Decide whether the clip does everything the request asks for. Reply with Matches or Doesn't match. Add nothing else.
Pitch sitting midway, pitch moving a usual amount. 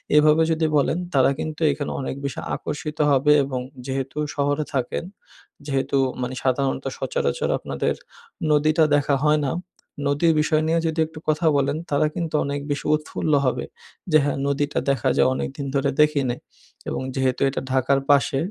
Doesn't match